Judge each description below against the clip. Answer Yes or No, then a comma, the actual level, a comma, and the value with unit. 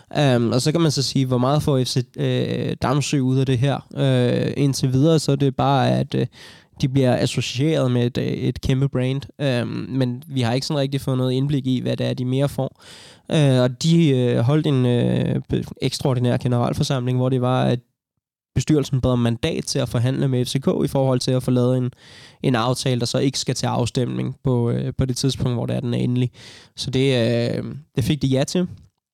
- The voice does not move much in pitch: Yes, narrow, 1.8 semitones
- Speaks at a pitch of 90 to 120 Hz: No, low, 130 Hz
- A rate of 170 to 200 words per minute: No, average, 220 wpm